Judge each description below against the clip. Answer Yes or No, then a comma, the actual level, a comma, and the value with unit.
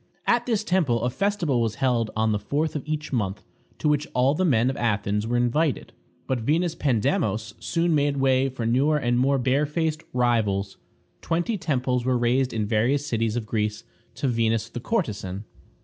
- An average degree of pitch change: Yes, average, 4.8 semitones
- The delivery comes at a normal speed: Yes, average, 180 wpm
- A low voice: Yes, low, 125 Hz